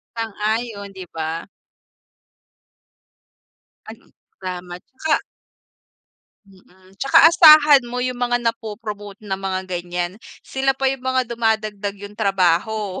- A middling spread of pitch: Yes, average, 4.4 semitones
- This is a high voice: Yes, high, 215 Hz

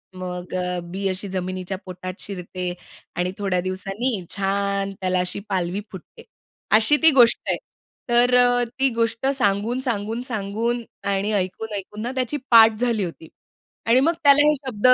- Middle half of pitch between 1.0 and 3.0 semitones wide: No, average, 4.3 semitones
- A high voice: Yes, high, 200 Hz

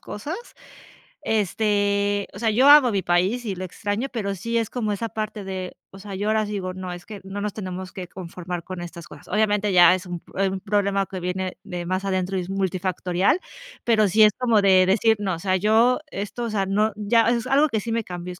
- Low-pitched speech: No, high, 200 Hz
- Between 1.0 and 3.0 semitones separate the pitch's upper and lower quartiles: Yes, average, 2.7 semitones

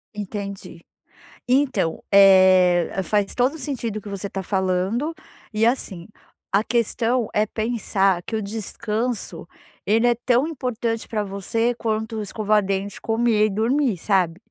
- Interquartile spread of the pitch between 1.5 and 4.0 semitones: Yes, average, 3.2 semitones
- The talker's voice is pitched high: Yes, high, 215 Hz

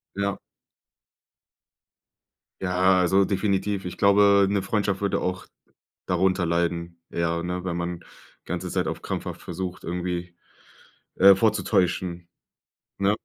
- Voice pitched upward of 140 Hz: No, very low, 90 Hz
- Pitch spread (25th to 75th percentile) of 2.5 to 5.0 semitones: No, narrow, 2.1 semitones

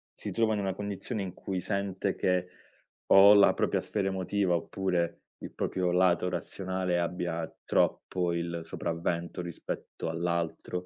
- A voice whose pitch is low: Yes, very low, 90 Hz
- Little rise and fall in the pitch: Yes, narrow, 2.1 semitones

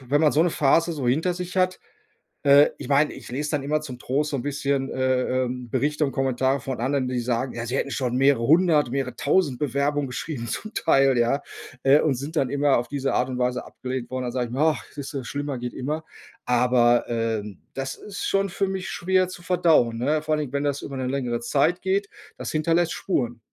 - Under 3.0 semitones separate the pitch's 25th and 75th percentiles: No, average, 3.4 semitones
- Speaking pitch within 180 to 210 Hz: No, medium, 140 Hz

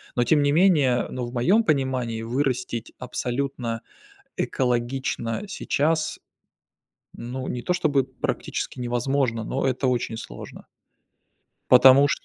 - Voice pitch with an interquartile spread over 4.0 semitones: No, narrow, 2.6 semitones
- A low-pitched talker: Yes, low, 130 Hz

